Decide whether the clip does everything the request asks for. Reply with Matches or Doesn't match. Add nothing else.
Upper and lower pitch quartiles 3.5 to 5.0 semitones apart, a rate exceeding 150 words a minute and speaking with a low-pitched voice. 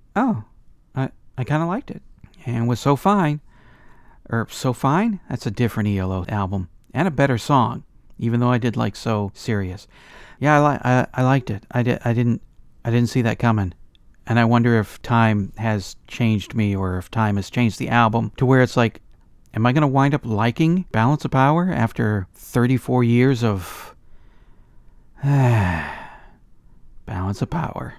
Matches